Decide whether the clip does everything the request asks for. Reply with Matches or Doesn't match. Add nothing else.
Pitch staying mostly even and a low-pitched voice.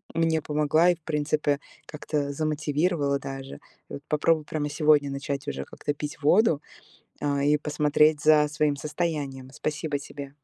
Doesn't match